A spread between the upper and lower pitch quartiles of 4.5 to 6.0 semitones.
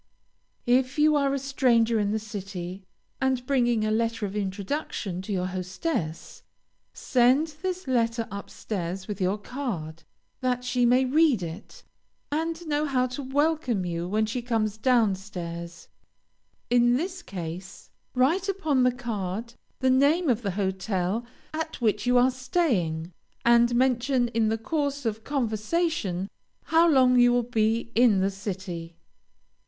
Yes: average, 5.1 semitones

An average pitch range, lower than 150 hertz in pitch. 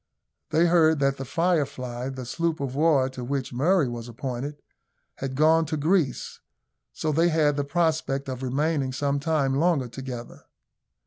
Yes: average, 3.4 semitones; medium, 140 Hz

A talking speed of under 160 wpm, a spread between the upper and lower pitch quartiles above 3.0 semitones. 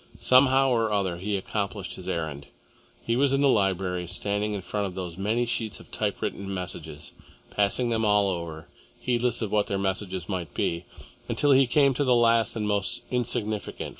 No: average, 180 wpm; average, 4.2 semitones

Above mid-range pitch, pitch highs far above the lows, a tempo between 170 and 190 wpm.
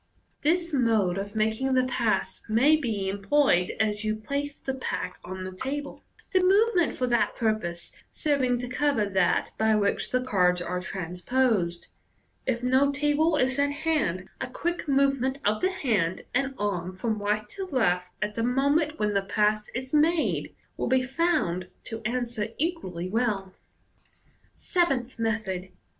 No: high, 240 Hz; wide, 5.9 semitones; average, 160 wpm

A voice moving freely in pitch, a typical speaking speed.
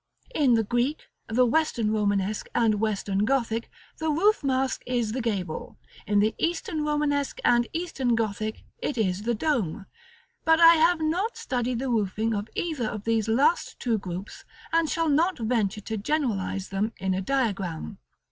Yes: wide, 5.9 semitones; average, 165 wpm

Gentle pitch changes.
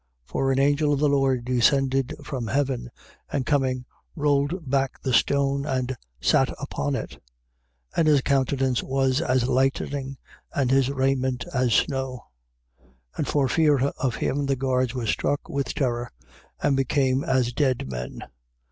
Yes: narrow, 1.6 semitones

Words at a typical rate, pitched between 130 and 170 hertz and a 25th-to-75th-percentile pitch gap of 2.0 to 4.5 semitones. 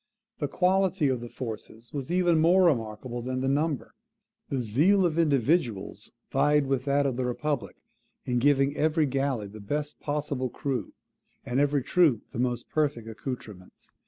Yes: average, 160 wpm; low, 135 Hz; average, 3.7 semitones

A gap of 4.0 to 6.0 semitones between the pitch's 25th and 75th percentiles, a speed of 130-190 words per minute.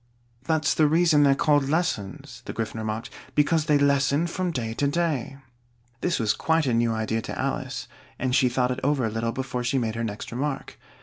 No: average, 4.4 semitones; average, 200 wpm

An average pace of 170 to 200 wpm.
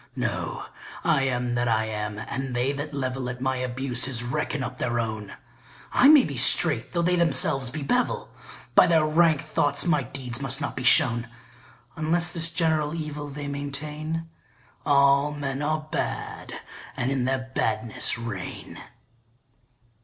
No: average, 155 wpm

